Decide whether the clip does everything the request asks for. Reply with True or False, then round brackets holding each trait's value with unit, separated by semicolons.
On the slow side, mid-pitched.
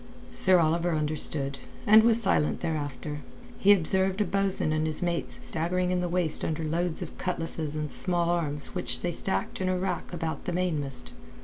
False (180 wpm; 170 Hz)